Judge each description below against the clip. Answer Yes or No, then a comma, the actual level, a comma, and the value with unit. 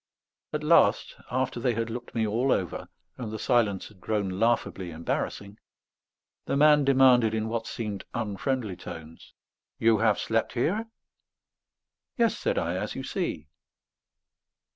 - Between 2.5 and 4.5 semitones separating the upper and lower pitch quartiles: Yes, average, 3.7 semitones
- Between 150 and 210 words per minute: No, average, 140 wpm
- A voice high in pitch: No, low, 115 Hz